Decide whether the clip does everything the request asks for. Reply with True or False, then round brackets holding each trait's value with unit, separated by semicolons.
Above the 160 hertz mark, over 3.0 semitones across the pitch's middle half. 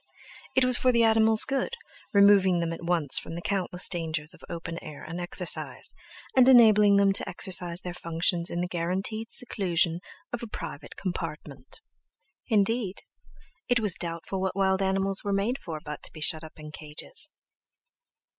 True (185 Hz; 3.9 semitones)